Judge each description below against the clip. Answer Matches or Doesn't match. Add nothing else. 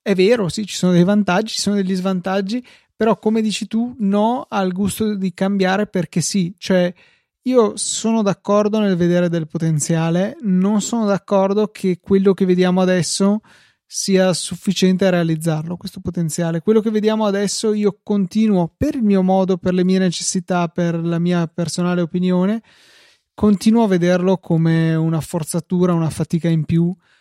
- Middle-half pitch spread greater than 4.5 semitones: Doesn't match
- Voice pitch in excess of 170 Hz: Matches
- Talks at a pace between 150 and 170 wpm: Matches